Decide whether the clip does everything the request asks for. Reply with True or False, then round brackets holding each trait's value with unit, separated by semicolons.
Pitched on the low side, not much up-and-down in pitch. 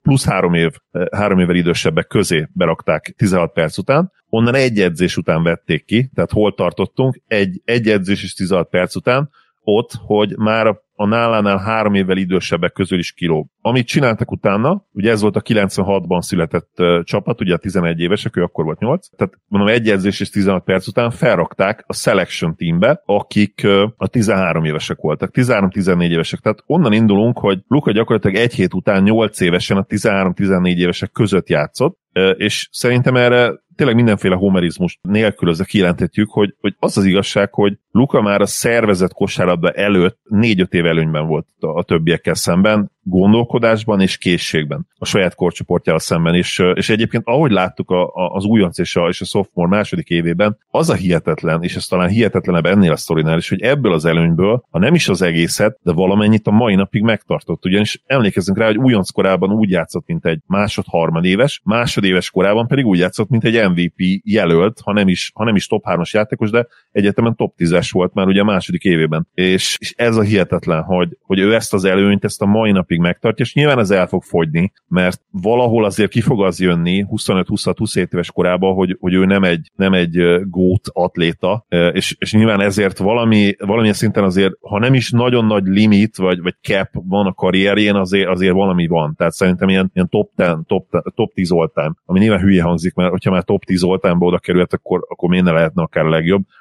False (100 Hz; 3.2 semitones)